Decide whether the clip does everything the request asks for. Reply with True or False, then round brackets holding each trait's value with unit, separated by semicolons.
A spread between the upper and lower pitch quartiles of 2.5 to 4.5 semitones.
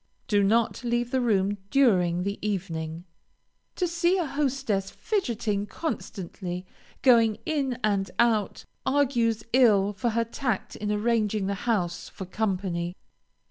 True (4.0 semitones)